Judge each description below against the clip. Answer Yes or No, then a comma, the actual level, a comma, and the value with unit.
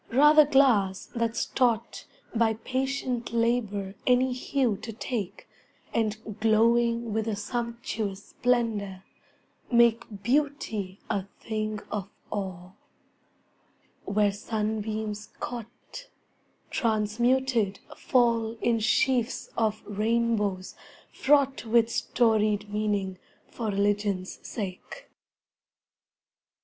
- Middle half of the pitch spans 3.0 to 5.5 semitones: No, narrow, 2.5 semitones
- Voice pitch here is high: Yes, high, 220 Hz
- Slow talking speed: Yes, slow, 90 wpm